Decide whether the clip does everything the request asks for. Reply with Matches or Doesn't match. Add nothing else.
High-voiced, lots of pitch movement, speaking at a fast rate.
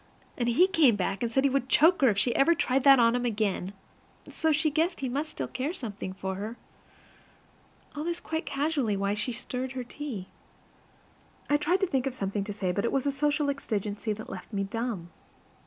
Matches